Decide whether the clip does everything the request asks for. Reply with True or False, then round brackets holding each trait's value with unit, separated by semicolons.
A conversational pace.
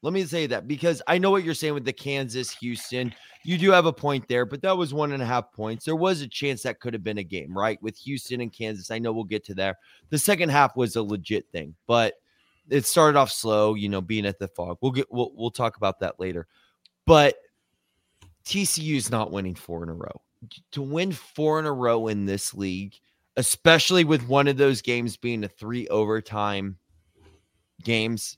False (220 wpm)